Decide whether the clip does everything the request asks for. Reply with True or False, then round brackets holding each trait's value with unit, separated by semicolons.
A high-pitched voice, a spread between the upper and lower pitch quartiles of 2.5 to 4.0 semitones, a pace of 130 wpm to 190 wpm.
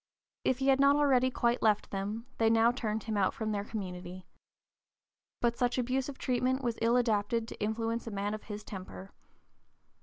True (225 Hz; 3.1 semitones; 180 wpm)